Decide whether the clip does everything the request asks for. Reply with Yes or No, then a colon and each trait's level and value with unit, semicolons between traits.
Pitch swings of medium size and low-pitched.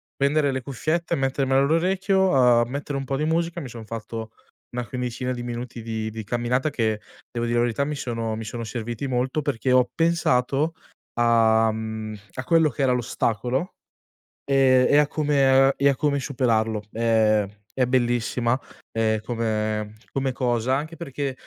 Yes: average, 3.5 semitones; low, 125 Hz